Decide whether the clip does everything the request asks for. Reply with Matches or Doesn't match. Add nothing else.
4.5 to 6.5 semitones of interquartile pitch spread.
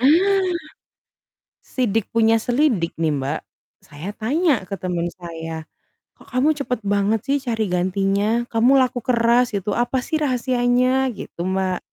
Matches